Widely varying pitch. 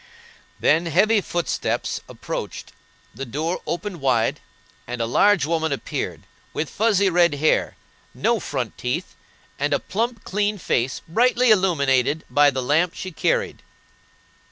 Yes: wide, 6.3 semitones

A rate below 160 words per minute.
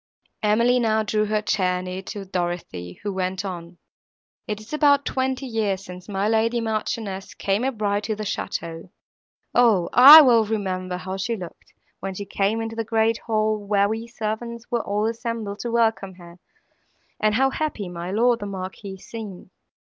No: average, 170 wpm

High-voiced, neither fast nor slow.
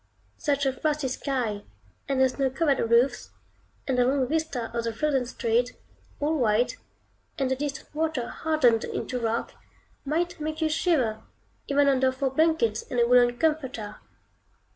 Yes: very high, 265 Hz; average, 155 wpm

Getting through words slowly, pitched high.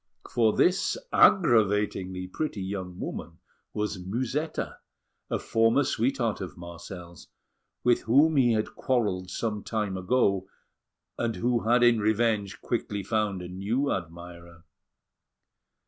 No: slow, 115 wpm; low, 105 Hz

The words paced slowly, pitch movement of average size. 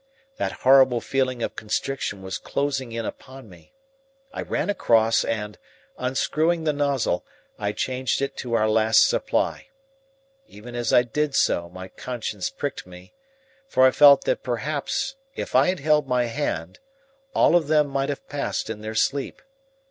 No: average, 160 wpm; average, 4.4 semitones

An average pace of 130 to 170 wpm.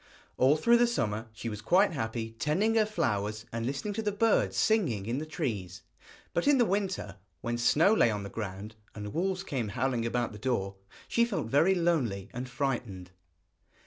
No: average, 185 wpm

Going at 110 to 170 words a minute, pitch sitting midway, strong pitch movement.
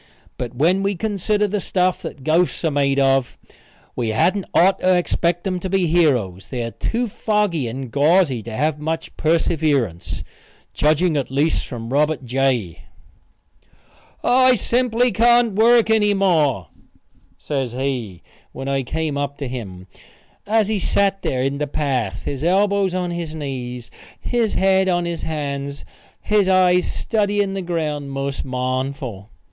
Yes: average, 150 wpm; medium, 155 Hz; wide, 6.2 semitones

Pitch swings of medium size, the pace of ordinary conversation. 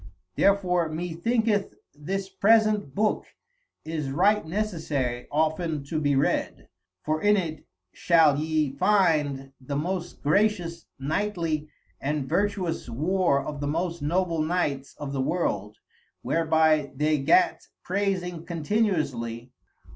No: average, 4.5 semitones; slow, 115 wpm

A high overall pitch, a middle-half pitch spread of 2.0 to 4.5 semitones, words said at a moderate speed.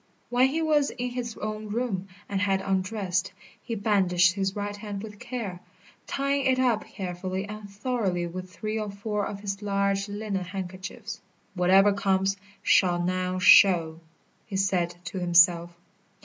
Yes: high, 200 Hz; narrow, 2.6 semitones; average, 150 wpm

